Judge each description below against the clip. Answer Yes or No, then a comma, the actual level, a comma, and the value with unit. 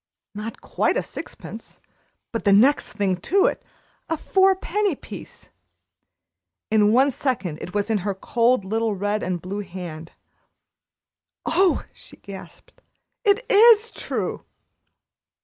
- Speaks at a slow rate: Yes, slow, 130 wpm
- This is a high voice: Yes, high, 220 Hz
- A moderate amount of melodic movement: No, wide, 8.9 semitones